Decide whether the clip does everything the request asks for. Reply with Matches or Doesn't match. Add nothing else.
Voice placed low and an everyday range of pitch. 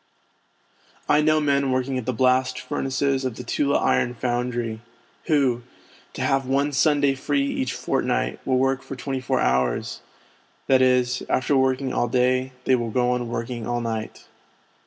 Doesn't match